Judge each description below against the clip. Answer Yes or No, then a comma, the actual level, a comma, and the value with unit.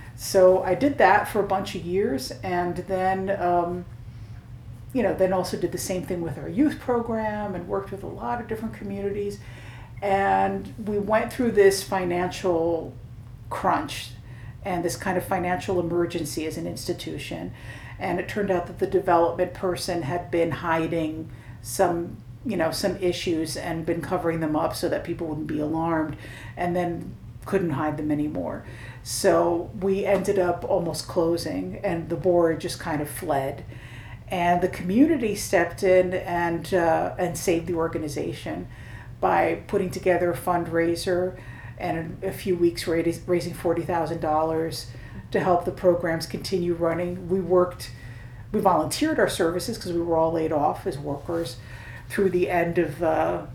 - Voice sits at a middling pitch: Yes, medium, 170 Hz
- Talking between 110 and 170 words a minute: Yes, average, 160 wpm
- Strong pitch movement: No, average, 3.7 semitones